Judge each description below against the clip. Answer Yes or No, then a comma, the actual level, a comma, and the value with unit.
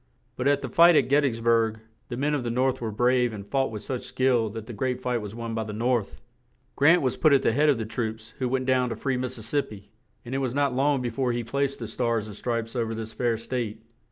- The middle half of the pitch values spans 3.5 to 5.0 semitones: No, average, 2.8 semitones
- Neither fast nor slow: No, fast, 270 wpm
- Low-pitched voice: Yes, low, 120 Hz